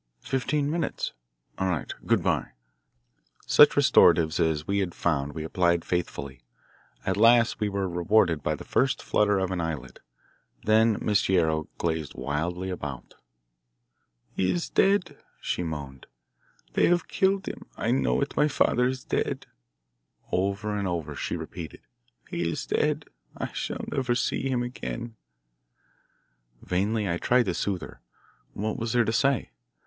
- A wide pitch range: Yes, wide, 6.4 semitones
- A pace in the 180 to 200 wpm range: No, average, 150 wpm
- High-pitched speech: No, very low, 95 Hz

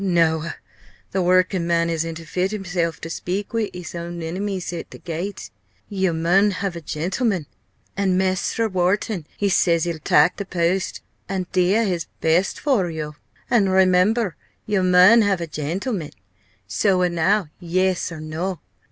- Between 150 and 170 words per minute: Yes, average, 155 wpm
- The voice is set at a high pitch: No, medium, 180 Hz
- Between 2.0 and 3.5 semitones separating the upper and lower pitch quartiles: Yes, narrow, 2.6 semitones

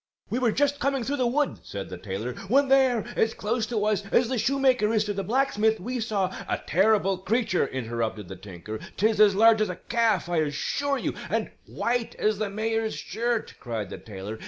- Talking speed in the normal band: No, fast, 210 wpm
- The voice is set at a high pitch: Yes, high, 215 Hz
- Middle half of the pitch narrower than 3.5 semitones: No, average, 5.2 semitones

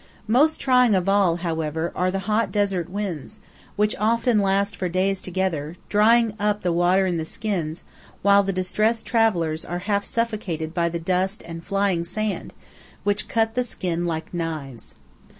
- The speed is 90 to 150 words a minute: No, average, 165 wpm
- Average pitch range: Yes, average, 3.7 semitones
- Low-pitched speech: No, high, 190 Hz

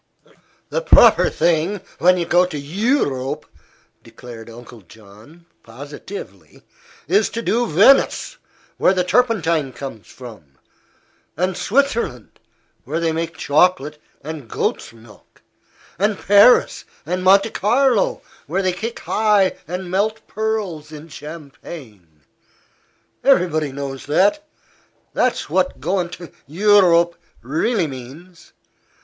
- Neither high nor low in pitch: Yes, medium, 170 Hz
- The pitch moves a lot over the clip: Yes, wide, 6.3 semitones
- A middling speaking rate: No, slow, 115 wpm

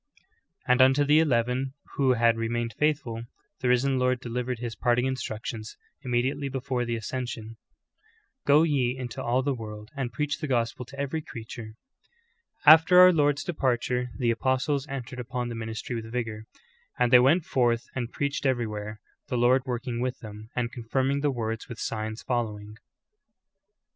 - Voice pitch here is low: Yes, low, 125 Hz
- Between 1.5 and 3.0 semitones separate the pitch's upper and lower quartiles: Yes, narrow, 2.6 semitones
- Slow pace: No, average, 165 wpm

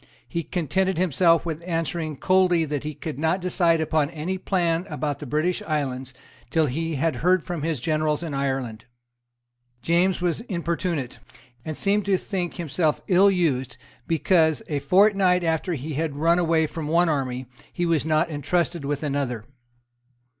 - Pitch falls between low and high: Yes, medium, 165 Hz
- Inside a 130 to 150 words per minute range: No, average, 160 wpm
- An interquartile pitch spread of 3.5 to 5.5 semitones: No, average, 3.1 semitones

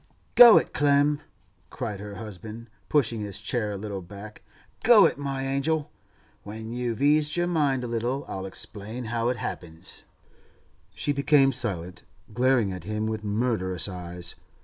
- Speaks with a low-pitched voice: Yes, low, 115 Hz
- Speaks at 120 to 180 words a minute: Yes, average, 150 wpm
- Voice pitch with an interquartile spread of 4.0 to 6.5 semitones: Yes, average, 5.2 semitones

